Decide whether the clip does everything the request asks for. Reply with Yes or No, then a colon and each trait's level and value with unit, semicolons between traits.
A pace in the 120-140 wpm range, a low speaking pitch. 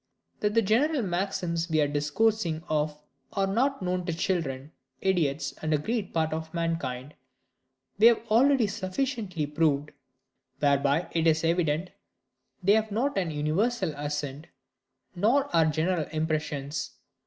No: slow, 135 wpm; medium, 165 Hz